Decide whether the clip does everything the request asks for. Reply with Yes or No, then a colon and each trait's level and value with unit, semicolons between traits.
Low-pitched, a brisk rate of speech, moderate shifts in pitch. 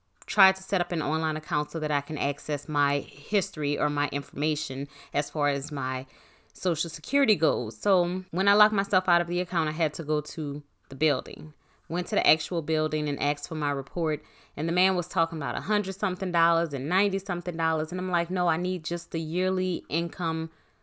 No: medium, 160 Hz; fast, 215 wpm; average, 3.6 semitones